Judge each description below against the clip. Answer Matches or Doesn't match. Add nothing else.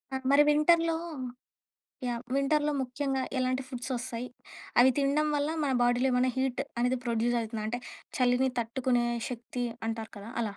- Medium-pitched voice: Doesn't match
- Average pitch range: Doesn't match